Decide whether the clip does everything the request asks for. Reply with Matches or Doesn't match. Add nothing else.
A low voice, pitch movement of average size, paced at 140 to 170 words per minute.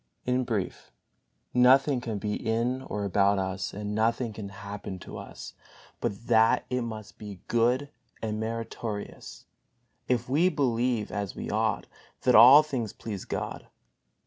Matches